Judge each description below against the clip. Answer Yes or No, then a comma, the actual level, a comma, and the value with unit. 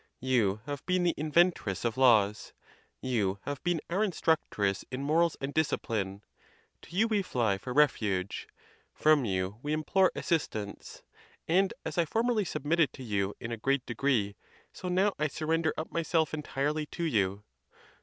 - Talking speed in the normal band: Yes, average, 165 wpm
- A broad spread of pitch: Yes, wide, 7.5 semitones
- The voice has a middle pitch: Yes, medium, 145 Hz